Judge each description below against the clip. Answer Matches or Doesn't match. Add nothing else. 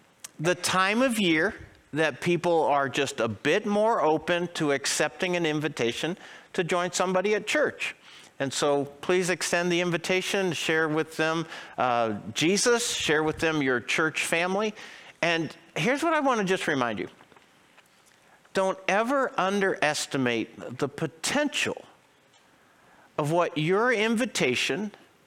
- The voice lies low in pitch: Doesn't match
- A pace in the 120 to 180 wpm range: Matches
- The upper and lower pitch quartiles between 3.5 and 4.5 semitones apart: Matches